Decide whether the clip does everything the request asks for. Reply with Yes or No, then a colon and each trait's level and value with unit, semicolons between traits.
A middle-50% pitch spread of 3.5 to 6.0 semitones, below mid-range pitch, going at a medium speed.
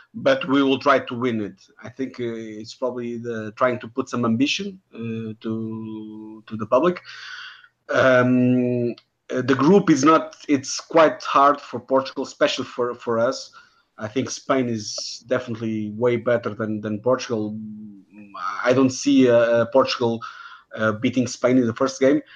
No: average, 3.0 semitones; low, 125 Hz; average, 160 wpm